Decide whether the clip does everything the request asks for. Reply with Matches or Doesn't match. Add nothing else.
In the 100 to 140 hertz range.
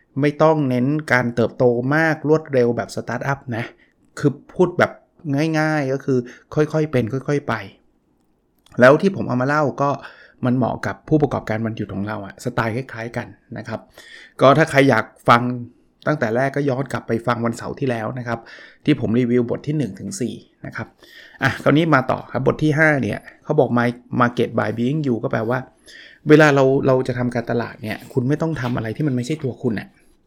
Matches